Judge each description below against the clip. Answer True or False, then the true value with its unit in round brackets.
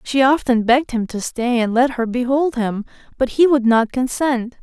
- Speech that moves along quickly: True (210 wpm)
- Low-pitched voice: False (250 Hz)